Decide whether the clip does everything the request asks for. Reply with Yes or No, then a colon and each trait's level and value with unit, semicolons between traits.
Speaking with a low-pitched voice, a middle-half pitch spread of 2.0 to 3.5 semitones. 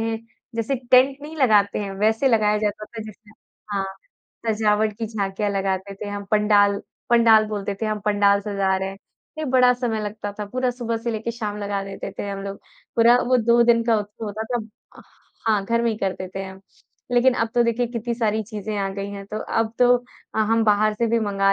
No: high, 215 Hz; narrow, 2.4 semitones